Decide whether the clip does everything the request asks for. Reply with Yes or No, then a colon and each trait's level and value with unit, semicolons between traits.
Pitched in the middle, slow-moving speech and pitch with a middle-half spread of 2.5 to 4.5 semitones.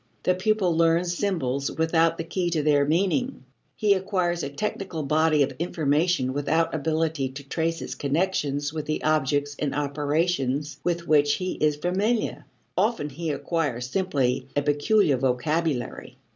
No: medium, 155 Hz; average, 145 wpm; average, 3.5 semitones